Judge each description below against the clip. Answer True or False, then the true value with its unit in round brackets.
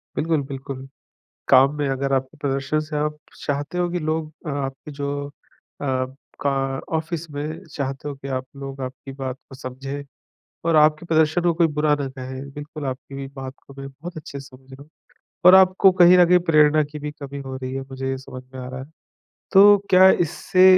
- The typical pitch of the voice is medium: True (145 Hz)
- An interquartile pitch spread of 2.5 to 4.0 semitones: True (2.8 semitones)